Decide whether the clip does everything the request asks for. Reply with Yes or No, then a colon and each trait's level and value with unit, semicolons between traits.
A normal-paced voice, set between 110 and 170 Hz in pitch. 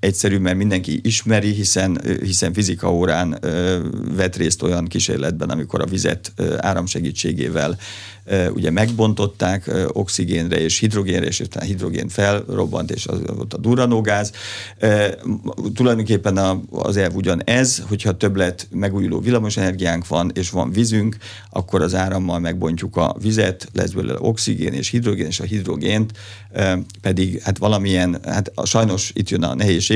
No: average, 140 wpm; very low, 95 Hz